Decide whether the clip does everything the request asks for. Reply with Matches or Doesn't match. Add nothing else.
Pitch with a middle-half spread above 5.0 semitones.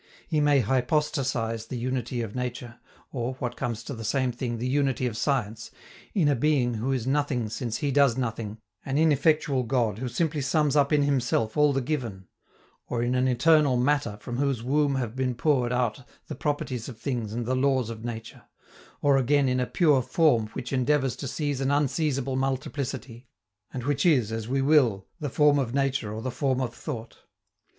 Doesn't match